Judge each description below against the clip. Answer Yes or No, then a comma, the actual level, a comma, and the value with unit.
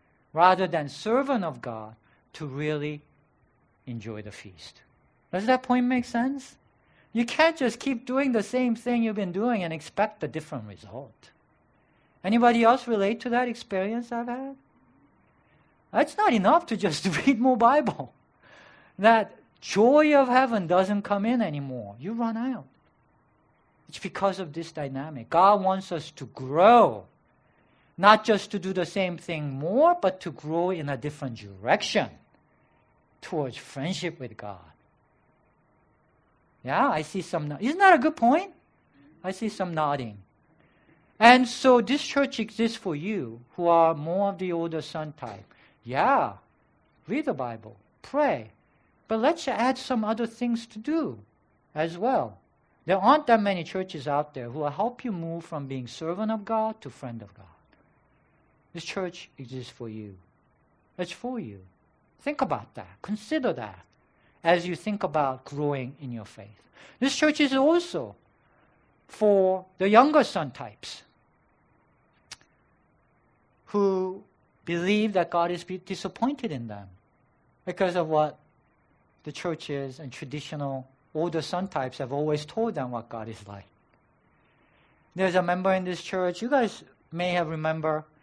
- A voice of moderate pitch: Yes, medium, 180 Hz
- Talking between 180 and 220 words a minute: No, average, 150 wpm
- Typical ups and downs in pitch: No, wide, 8.2 semitones